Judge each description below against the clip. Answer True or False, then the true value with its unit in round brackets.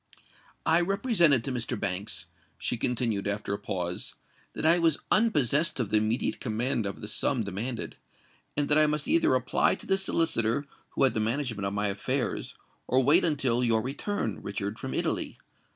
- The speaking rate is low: False (175 wpm)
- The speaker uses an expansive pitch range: True (6.3 semitones)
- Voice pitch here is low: True (120 Hz)